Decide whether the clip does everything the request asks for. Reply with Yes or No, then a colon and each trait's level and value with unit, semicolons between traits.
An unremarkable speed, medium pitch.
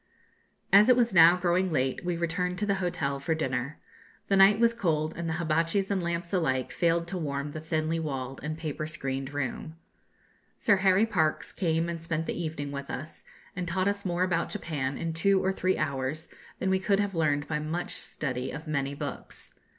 Yes: average, 195 wpm; medium, 165 Hz